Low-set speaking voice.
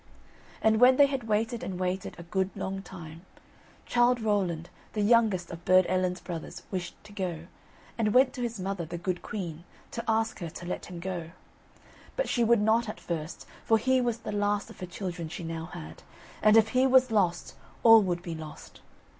No: high, 195 Hz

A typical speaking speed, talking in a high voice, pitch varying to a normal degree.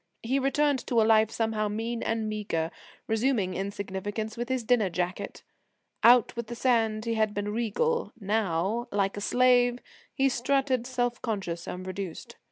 Yes: average, 160 wpm; high, 220 Hz; average, 3.3 semitones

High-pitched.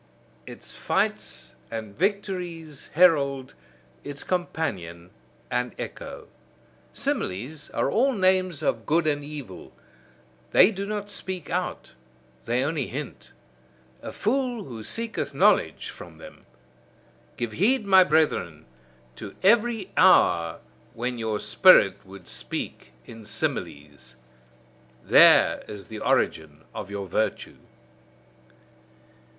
No: medium, 145 Hz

